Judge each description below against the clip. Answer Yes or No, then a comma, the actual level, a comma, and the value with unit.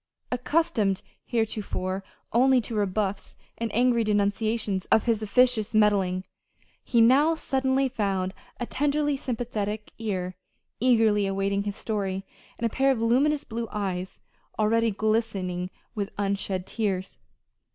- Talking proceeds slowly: Yes, slow, 120 wpm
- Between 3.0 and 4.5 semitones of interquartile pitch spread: Yes, average, 3.6 semitones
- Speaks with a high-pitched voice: Yes, high, 215 Hz